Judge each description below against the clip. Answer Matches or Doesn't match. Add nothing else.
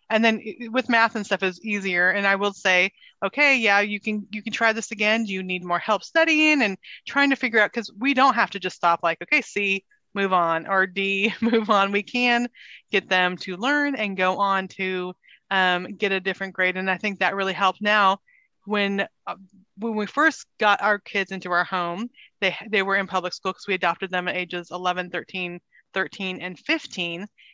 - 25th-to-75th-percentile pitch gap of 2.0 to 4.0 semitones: Matches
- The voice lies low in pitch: Doesn't match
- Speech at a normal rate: Doesn't match